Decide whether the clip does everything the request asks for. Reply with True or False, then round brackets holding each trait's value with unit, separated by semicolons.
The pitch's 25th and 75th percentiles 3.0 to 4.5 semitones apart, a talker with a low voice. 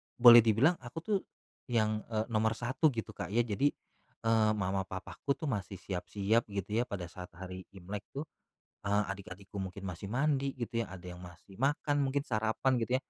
True (4.1 semitones; 110 Hz)